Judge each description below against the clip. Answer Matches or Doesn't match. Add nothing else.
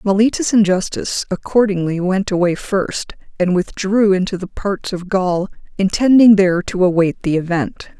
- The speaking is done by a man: Doesn't match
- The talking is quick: Doesn't match